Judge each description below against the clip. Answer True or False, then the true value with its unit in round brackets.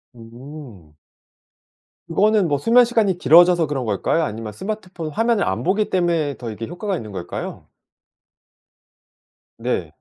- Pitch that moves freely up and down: True (8.8 semitones)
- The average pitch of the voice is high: False (160 Hz)